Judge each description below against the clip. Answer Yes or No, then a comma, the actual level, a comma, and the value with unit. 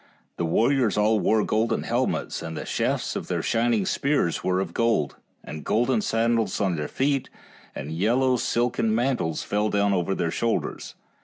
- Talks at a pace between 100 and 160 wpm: No, average, 170 wpm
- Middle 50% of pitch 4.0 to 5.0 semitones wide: Yes, average, 4.3 semitones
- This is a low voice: Yes, low, 110 Hz